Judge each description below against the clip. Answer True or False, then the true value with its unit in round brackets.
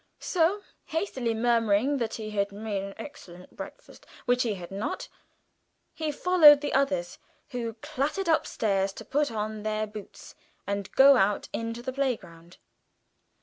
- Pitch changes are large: True (5.7 semitones)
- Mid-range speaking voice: False (230 Hz)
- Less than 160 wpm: True (145 wpm)